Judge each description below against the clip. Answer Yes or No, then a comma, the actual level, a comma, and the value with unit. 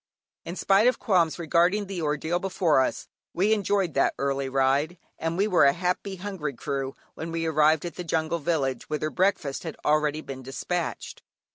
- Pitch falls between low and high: Yes, medium, 165 Hz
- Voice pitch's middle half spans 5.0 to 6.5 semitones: No, average, 3.9 semitones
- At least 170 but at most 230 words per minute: Yes, average, 175 wpm